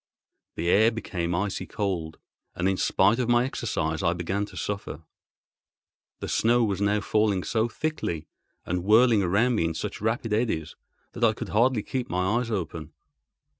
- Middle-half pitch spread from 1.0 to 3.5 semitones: No, average, 4.6 semitones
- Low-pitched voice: Yes, low, 105 Hz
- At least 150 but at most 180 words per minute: Yes, average, 170 wpm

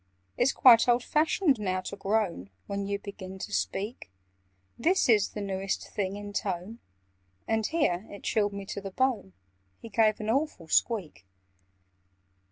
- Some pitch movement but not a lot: Yes, average, 3.2 semitones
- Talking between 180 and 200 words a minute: No, average, 155 wpm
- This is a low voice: No, high, 205 Hz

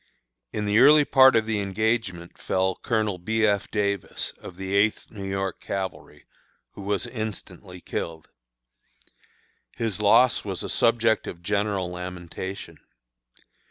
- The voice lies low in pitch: Yes, low, 100 Hz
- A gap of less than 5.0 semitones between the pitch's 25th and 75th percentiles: Yes, average, 2.9 semitones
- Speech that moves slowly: Yes, slow, 130 wpm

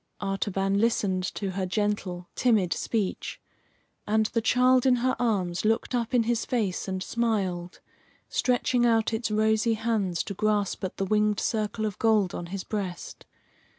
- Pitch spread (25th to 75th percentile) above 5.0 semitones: No, average, 3.0 semitones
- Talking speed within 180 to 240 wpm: No, average, 155 wpm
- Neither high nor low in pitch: No, high, 215 Hz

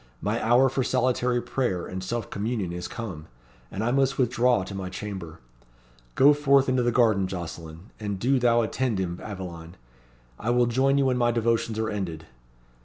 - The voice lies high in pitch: No, low, 115 Hz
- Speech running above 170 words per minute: Yes, average, 180 wpm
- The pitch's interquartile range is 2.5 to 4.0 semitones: No, average, 5.1 semitones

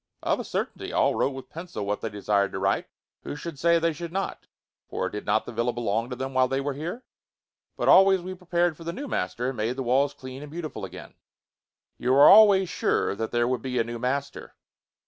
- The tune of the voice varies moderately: No, wide, 6.2 semitones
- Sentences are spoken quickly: Yes, fast, 225 wpm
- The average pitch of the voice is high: No, low, 135 Hz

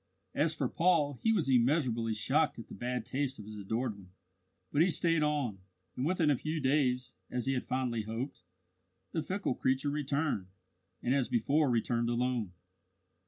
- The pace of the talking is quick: No, average, 170 wpm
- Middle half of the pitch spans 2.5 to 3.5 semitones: No, average, 4.1 semitones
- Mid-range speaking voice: No, low, 130 Hz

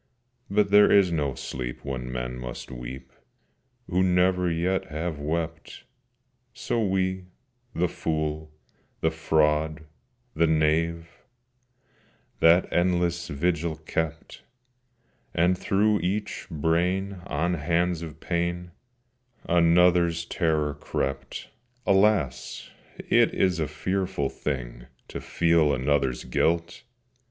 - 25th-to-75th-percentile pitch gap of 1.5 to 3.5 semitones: Yes, average, 3.0 semitones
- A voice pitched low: Yes, very low, 85 Hz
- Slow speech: Yes, slow, 100 wpm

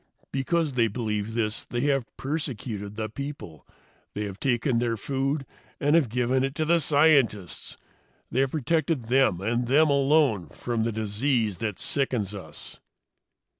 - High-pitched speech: No, low, 125 Hz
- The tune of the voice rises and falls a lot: No, average, 4.6 semitones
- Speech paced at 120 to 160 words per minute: Yes, average, 150 wpm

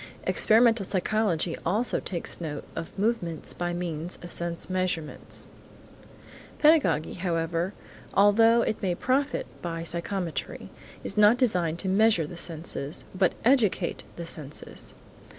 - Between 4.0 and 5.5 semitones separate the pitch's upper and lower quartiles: Yes, average, 4.3 semitones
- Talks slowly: Yes, slow, 120 wpm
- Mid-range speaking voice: Yes, medium, 180 Hz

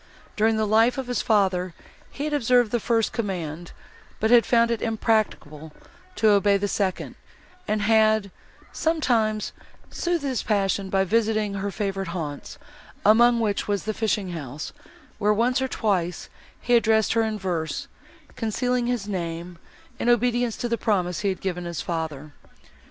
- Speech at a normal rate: Yes, average, 155 wpm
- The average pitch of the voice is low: No, high, 215 Hz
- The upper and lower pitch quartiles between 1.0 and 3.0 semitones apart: No, average, 3.7 semitones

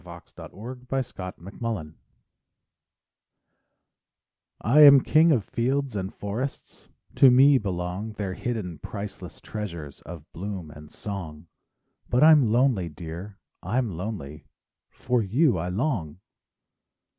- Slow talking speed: Yes, slow, 120 wpm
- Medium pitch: No, low, 105 Hz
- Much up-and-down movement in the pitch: Yes, wide, 6.2 semitones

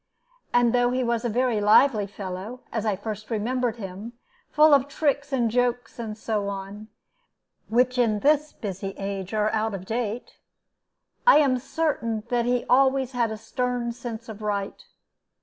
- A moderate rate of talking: Yes, average, 165 wpm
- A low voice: No, high, 230 Hz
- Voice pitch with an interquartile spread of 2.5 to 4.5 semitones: Yes, average, 2.9 semitones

